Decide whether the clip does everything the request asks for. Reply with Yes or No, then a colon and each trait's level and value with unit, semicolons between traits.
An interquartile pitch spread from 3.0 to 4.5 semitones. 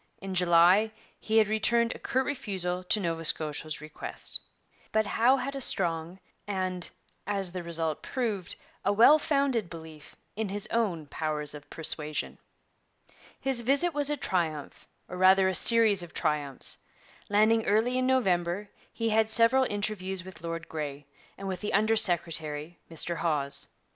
No: average, 5.1 semitones